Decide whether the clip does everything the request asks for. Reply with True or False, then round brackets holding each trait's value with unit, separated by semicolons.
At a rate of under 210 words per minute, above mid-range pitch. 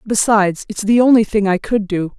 False (220 wpm; 210 Hz)